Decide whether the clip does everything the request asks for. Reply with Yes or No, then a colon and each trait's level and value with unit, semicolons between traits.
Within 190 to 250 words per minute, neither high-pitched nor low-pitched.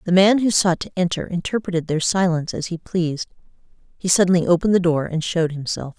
Yes: average, 200 wpm; medium, 175 Hz